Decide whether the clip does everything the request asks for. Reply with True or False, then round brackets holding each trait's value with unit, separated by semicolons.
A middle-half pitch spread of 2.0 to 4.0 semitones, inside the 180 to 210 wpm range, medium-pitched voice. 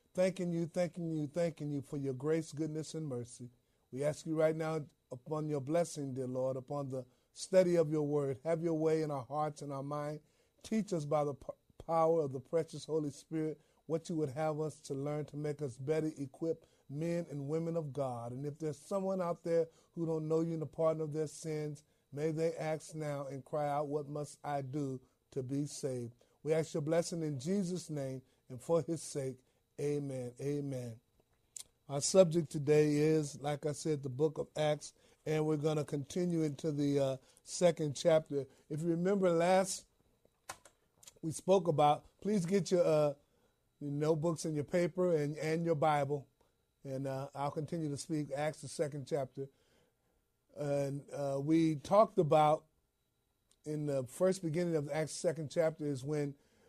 True (2.4 semitones; 185 wpm; 150 Hz)